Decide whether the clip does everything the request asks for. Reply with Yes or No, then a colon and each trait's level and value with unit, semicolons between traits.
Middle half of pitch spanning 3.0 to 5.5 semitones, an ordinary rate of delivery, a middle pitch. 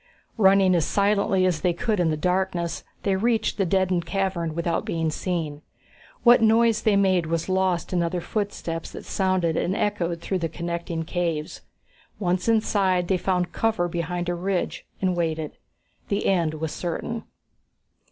No: narrow, 2.5 semitones; average, 160 wpm; medium, 180 Hz